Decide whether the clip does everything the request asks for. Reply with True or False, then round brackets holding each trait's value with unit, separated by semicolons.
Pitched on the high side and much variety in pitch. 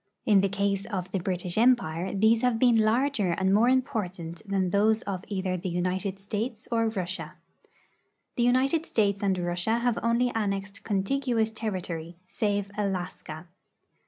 False (200 Hz; 3.5 semitones)